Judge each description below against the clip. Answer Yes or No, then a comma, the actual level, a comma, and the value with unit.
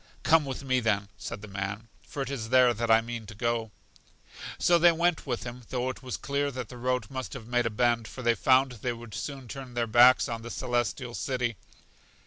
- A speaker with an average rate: No, fast, 225 wpm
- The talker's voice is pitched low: Yes, low, 120 Hz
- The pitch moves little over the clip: Yes, narrow, 2.2 semitones